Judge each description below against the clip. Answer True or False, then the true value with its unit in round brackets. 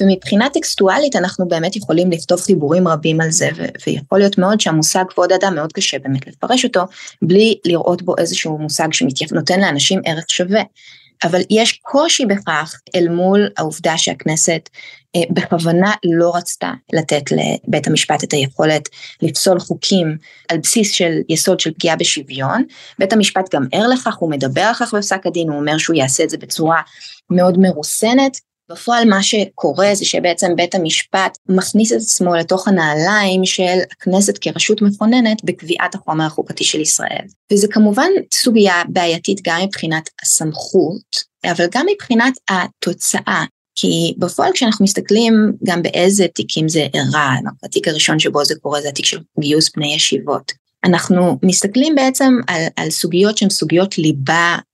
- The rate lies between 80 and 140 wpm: False (150 wpm)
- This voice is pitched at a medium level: True (180 Hz)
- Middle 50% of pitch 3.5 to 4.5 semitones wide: True (4.0 semitones)